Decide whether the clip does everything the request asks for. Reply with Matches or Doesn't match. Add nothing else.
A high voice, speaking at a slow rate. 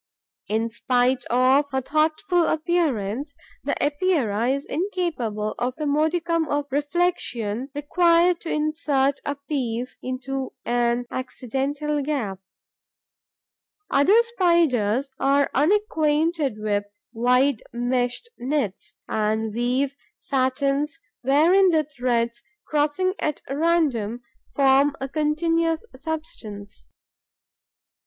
Matches